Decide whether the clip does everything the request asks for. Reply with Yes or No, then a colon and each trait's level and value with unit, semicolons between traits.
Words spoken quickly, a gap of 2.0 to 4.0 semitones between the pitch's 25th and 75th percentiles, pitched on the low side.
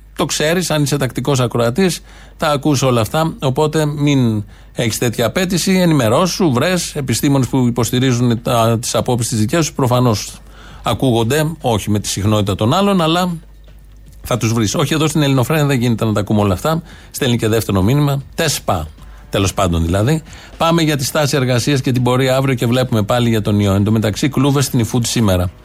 No: fast, 180 wpm; average, 5.1 semitones; low, 125 Hz